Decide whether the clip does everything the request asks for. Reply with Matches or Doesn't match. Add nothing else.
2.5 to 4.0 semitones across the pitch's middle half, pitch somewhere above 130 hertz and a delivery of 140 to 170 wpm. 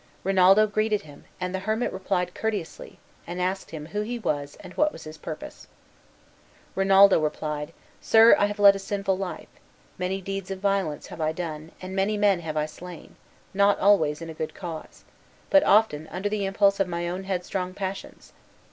Doesn't match